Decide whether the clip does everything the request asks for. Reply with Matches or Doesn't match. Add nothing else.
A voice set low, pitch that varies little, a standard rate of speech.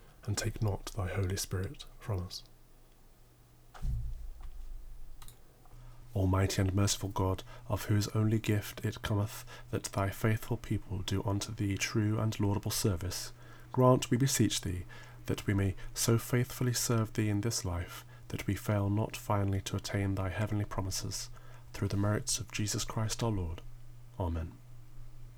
Doesn't match